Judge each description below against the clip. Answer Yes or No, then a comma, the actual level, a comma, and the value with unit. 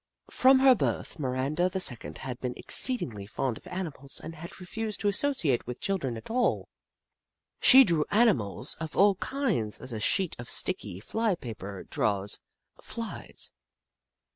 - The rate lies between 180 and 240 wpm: No, average, 150 wpm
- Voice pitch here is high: No, medium, 160 Hz